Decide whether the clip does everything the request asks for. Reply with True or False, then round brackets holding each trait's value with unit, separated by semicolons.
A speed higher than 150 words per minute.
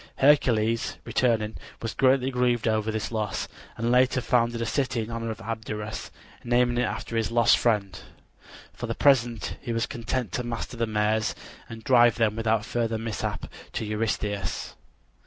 True (160 wpm)